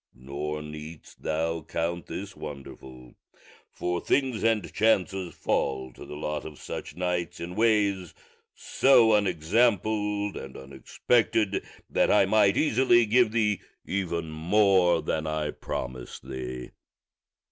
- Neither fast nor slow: No, slow, 120 wpm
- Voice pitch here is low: Yes, very low, 90 Hz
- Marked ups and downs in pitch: Yes, wide, 5.7 semitones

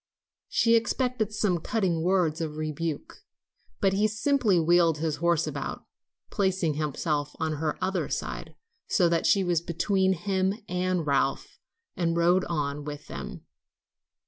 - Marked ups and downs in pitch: No, average, 3.5 semitones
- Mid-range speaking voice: Yes, medium, 175 Hz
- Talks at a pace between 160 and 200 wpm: No, average, 140 wpm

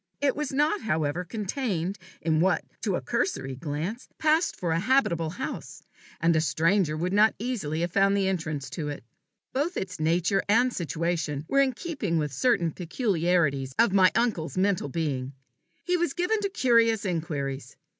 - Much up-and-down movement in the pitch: Yes, wide, 7.1 semitones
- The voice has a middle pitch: Yes, medium, 180 Hz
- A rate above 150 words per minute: Yes, average, 165 wpm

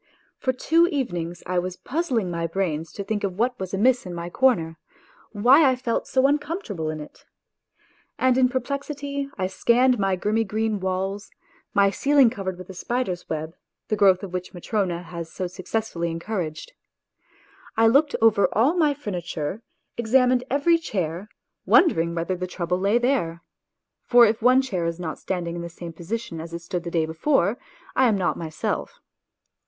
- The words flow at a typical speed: Yes, average, 180 wpm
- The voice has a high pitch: Yes, high, 200 Hz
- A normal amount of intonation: No, wide, 6.5 semitones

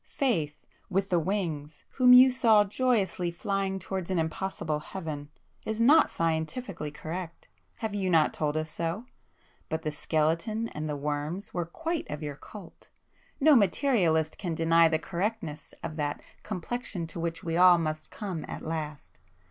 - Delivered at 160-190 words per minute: No, average, 150 wpm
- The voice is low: No, medium, 170 Hz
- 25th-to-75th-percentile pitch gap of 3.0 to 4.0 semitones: No, average, 4.7 semitones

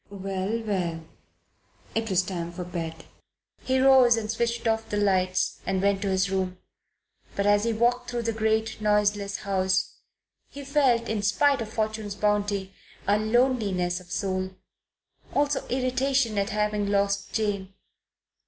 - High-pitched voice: Yes, high, 205 Hz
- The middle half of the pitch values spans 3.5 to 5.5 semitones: No, average, 3.0 semitones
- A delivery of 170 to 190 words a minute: No, average, 145 wpm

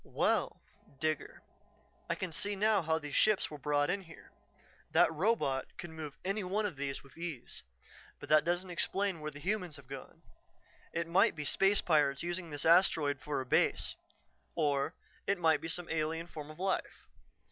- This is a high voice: No, medium, 165 Hz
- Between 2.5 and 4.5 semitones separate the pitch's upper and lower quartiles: Yes, average, 3.9 semitones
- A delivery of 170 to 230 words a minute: Yes, average, 180 wpm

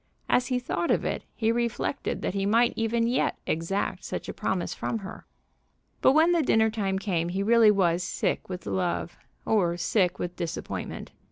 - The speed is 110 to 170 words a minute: No, average, 180 wpm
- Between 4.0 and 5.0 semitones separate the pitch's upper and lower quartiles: Yes, average, 4.4 semitones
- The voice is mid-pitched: No, high, 210 Hz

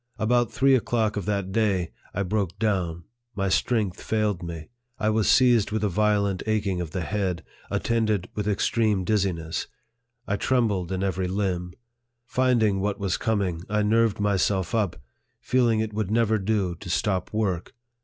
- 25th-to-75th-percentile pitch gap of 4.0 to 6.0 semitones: No, average, 2.8 semitones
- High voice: No, low, 105 Hz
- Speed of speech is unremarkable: Yes, average, 165 wpm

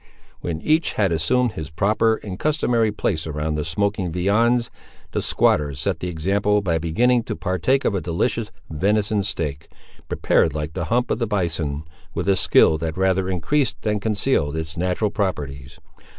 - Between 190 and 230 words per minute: No, average, 165 wpm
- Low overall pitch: Yes, very low, 95 Hz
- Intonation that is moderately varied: Yes, average, 5.0 semitones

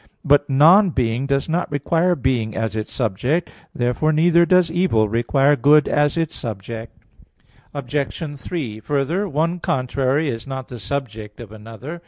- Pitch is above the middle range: No, medium, 140 Hz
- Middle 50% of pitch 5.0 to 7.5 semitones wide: Yes, wide, 5.5 semitones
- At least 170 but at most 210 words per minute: No, average, 150 wpm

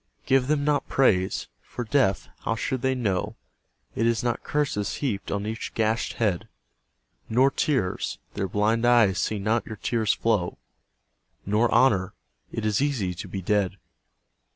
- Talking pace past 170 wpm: No, average, 150 wpm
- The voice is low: Yes, low, 110 Hz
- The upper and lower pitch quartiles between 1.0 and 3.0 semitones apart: No, average, 4.2 semitones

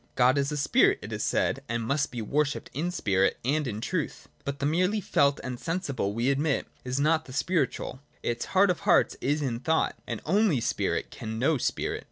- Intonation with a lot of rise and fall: No, average, 4.3 semitones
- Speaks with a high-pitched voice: No, medium, 140 Hz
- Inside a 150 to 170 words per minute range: No, fast, 205 wpm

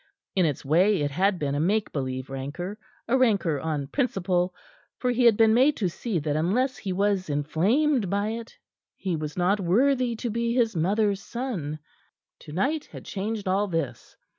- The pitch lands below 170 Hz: No, high, 195 Hz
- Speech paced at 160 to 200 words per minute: Yes, average, 175 wpm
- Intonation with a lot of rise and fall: Yes, wide, 6.2 semitones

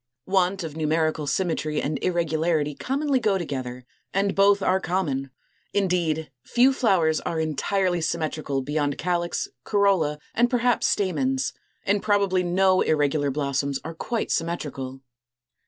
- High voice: No, medium, 165 Hz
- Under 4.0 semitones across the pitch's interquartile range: No, average, 4.5 semitones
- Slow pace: Yes, slow, 125 wpm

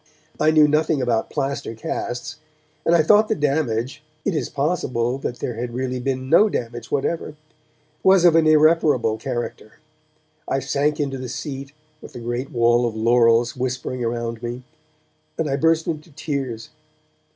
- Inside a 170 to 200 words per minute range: No, average, 160 wpm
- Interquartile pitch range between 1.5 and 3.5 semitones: No, average, 4.3 semitones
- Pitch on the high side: No, low, 135 Hz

